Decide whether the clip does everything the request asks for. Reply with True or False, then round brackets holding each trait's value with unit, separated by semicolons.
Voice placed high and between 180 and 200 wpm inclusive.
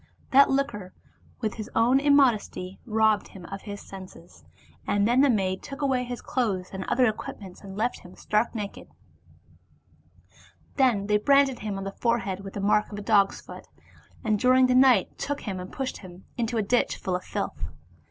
True (215 Hz; 190 wpm)